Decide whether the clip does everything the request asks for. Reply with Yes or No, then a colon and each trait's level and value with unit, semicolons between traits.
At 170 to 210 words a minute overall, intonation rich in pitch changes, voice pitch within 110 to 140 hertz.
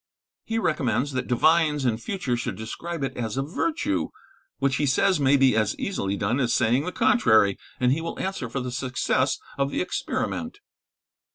Yes: average, 180 wpm; wide, 5.7 semitones; low, 135 Hz